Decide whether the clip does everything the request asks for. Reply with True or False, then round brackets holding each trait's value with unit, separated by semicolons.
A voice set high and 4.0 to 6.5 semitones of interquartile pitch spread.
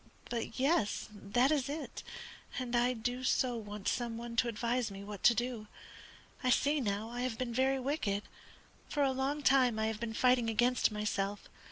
False (240 Hz; 2.9 semitones)